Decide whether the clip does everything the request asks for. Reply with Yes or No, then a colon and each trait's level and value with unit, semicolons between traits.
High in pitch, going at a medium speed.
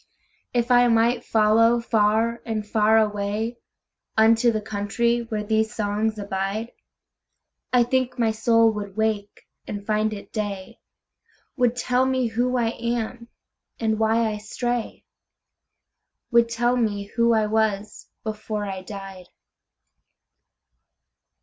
No: high, 220 Hz; slow, 110 wpm